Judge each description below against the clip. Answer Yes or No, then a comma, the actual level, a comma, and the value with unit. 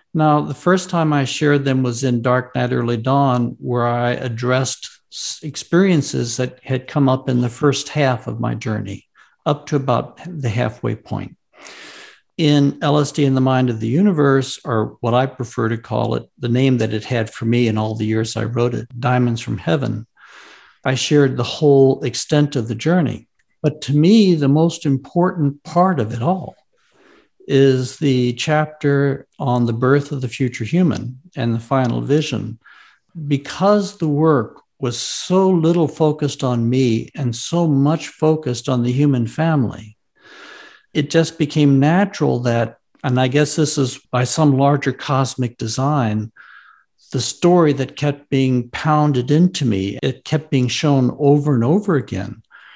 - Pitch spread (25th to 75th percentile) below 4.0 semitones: Yes, average, 3.6 semitones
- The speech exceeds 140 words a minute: Yes, average, 165 wpm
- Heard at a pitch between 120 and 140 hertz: Yes, low, 135 Hz